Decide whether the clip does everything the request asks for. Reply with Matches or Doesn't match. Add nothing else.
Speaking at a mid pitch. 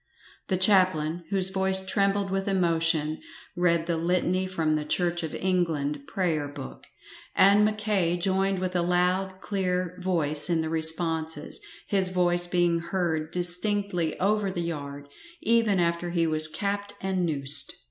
Matches